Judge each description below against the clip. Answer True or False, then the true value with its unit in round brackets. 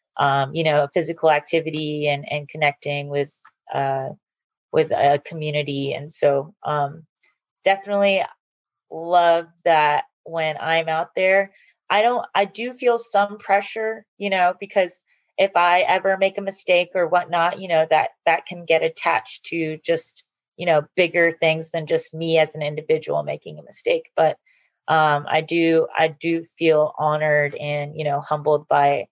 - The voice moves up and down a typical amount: True (3.9 semitones)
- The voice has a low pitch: False (165 Hz)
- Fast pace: False (155 wpm)